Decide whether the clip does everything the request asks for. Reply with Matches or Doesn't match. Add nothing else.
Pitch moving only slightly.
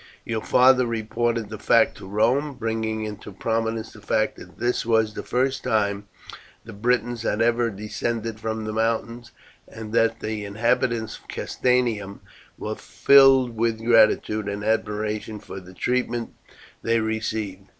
Matches